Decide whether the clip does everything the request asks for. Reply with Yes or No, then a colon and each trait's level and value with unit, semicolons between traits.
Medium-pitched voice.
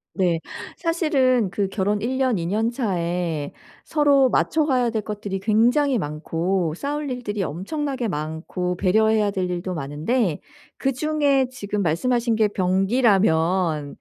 No: high, 210 Hz